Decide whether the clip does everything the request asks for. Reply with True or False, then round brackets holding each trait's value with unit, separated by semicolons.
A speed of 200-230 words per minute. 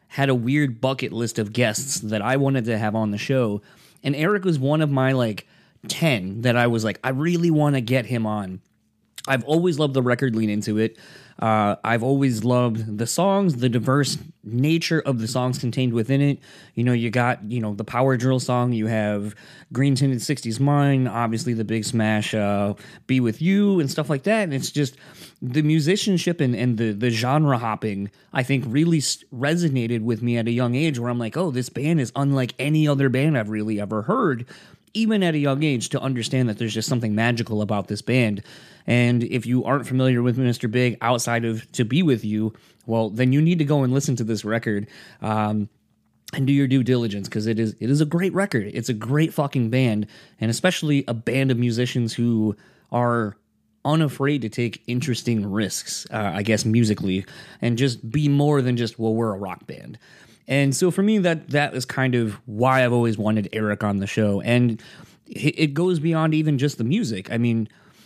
True (205 wpm)